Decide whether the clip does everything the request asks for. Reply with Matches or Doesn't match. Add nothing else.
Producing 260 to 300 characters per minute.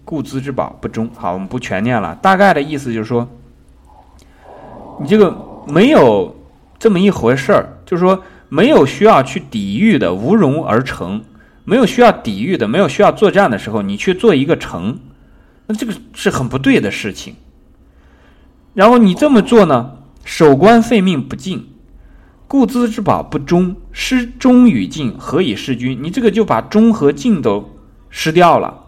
Doesn't match